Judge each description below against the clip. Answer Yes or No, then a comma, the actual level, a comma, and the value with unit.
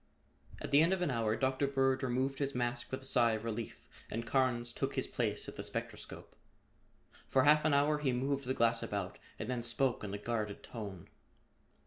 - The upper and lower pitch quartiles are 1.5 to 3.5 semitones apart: Yes, average, 3.0 semitones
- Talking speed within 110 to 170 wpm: No, average, 200 wpm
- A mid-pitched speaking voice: No, low, 125 Hz